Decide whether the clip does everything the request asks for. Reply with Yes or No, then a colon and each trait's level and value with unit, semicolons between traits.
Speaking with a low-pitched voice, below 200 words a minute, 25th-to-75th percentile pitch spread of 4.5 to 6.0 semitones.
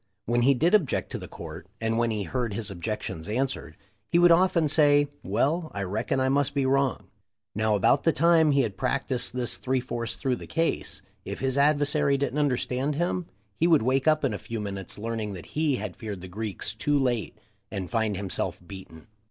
No: low, 130 Hz; fast, 205 wpm; average, 5.3 semitones